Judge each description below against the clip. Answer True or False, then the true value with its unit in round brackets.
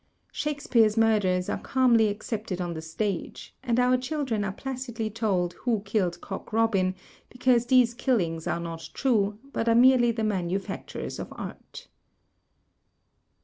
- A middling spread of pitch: True (4.5 semitones)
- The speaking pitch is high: True (220 Hz)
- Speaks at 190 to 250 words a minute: False (145 wpm)